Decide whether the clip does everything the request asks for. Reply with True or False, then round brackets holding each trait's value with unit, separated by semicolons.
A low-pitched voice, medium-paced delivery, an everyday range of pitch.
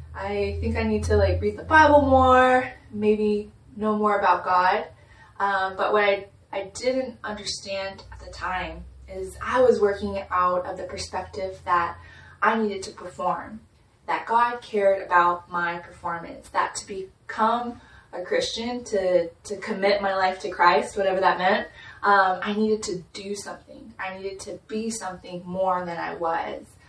False (195 Hz; 165 wpm; 3.3 semitones)